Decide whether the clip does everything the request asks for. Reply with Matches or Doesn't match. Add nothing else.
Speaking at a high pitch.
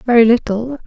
Matches